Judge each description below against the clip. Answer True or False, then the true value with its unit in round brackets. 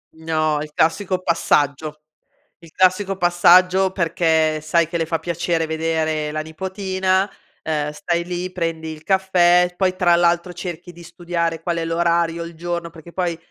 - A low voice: False (170 Hz)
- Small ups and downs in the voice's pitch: True (1.9 semitones)